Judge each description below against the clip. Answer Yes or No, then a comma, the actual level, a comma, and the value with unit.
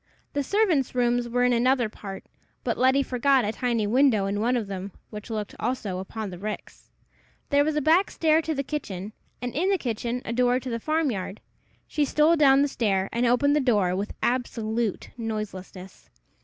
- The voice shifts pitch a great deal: No, average, 4.7 semitones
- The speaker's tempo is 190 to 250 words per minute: Yes, average, 195 wpm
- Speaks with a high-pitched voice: Yes, high, 245 Hz